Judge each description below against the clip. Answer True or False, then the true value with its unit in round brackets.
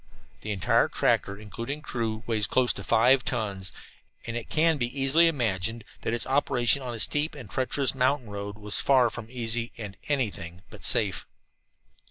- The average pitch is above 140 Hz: False (120 Hz)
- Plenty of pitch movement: False (3.9 semitones)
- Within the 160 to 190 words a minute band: True (175 wpm)